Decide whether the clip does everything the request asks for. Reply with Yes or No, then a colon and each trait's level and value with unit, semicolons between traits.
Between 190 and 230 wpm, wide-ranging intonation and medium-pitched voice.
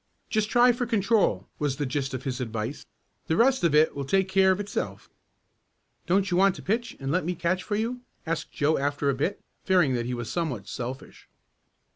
Yes: fast, 205 wpm; wide, 6.5 semitones; medium, 165 Hz